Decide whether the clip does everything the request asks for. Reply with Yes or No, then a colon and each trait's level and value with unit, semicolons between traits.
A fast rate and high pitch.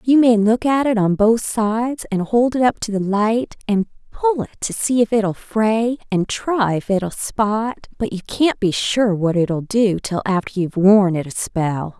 Yes: fast, 215 wpm; high, 215 Hz